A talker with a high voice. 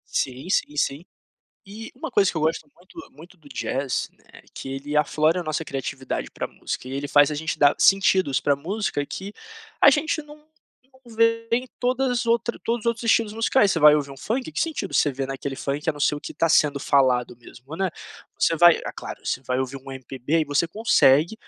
No: medium, 155 Hz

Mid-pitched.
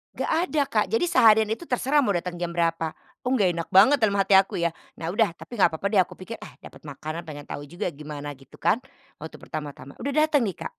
Yes: medium, 180 Hz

